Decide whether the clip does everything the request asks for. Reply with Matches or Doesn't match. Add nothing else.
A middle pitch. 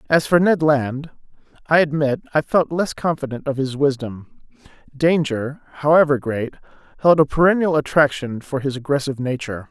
Matches